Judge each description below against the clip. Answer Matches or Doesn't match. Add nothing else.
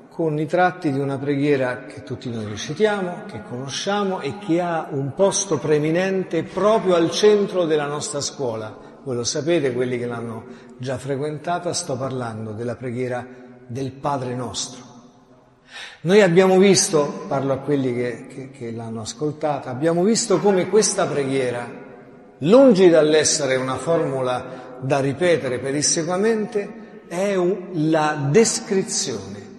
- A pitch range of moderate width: Doesn't match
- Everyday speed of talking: Matches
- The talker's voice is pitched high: Doesn't match